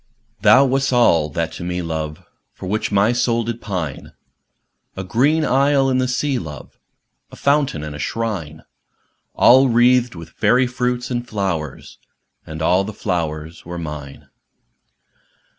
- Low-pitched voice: Yes, low, 105 Hz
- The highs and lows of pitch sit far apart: Yes, wide, 7.4 semitones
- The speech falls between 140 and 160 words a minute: Yes, average, 145 wpm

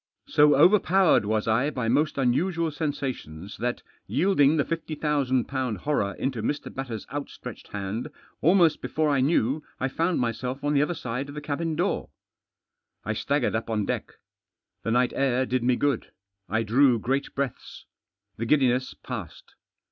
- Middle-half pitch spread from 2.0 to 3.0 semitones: No, average, 3.9 semitones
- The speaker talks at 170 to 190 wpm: No, average, 155 wpm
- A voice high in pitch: No, low, 135 Hz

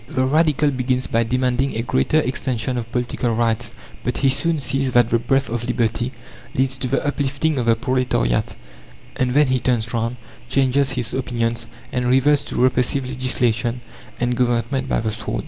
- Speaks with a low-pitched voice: Yes, low, 125 Hz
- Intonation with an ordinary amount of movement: No, narrow, 2.2 semitones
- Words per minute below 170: No, average, 175 wpm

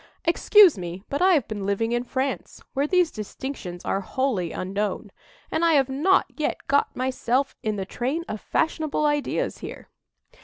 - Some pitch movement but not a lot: No, wide, 6.5 semitones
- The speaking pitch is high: Yes, very high, 265 Hz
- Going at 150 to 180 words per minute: Yes, average, 165 wpm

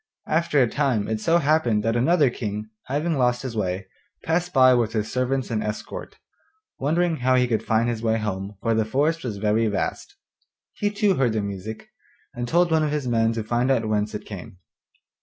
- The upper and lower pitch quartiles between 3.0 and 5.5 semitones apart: Yes, average, 5.0 semitones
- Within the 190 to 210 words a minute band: Yes, average, 200 wpm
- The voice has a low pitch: Yes, low, 120 Hz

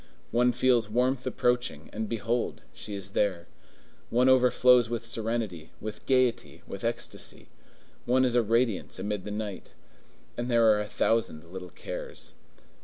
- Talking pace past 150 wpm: No, average, 145 wpm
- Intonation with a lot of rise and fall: No, average, 3.1 semitones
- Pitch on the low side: Yes, low, 115 Hz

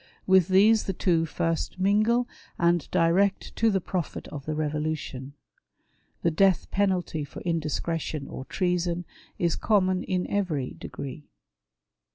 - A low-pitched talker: No, medium, 175 Hz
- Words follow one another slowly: Yes, slow, 130 wpm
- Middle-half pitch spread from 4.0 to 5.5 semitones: No, average, 3.6 semitones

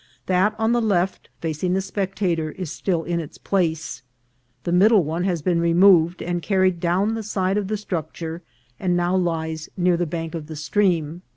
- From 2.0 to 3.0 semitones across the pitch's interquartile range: Yes, average, 2.7 semitones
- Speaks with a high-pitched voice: No, medium, 175 Hz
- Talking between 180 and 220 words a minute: Yes, average, 185 wpm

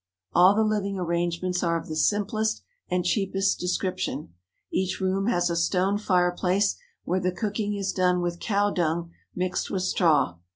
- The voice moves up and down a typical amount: No, narrow, 2.3 semitones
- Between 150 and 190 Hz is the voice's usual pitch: Yes, medium, 185 Hz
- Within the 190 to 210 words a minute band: No, average, 160 wpm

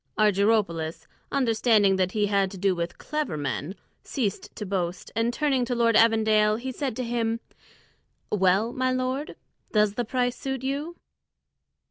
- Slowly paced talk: No, average, 150 wpm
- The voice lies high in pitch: Yes, high, 225 Hz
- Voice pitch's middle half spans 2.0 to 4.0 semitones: No, average, 4.4 semitones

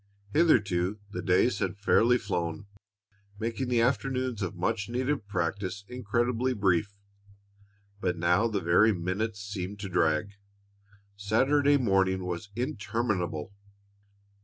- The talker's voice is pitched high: No, low, 100 Hz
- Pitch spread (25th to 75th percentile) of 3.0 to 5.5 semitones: Yes, average, 4.4 semitones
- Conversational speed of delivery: No, slow, 110 wpm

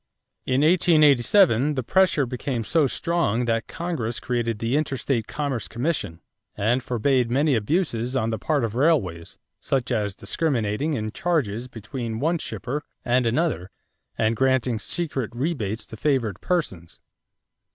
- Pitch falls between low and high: No, low, 125 Hz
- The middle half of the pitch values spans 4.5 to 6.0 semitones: Yes, average, 4.9 semitones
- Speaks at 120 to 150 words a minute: Yes, slow, 135 wpm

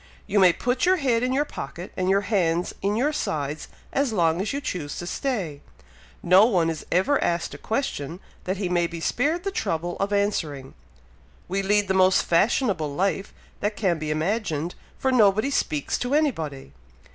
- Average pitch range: No, wide, 5.8 semitones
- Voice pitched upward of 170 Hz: Yes, high, 190 Hz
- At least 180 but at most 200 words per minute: Yes, average, 185 wpm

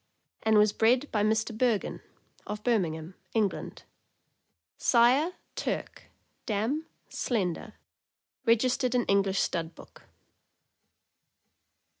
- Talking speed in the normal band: No, slow, 95 wpm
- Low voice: No, high, 220 Hz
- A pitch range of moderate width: Yes, average, 3.5 semitones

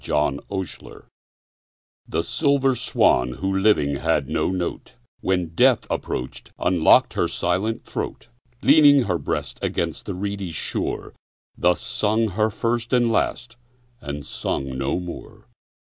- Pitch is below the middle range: Yes, very low, 95 Hz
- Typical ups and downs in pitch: No, wide, 5.7 semitones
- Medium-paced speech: No, slow, 130 wpm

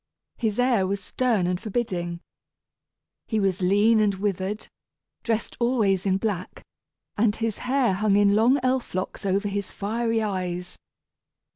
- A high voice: Yes, high, 205 Hz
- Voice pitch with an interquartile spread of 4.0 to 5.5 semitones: No, average, 3.2 semitones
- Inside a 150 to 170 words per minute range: No, average, 140 wpm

